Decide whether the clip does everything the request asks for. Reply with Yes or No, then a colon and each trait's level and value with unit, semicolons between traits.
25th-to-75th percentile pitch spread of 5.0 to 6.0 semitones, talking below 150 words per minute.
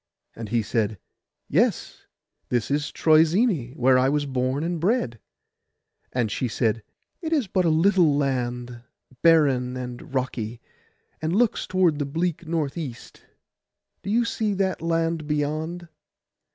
Yes: average, 5.3 semitones; average, 140 wpm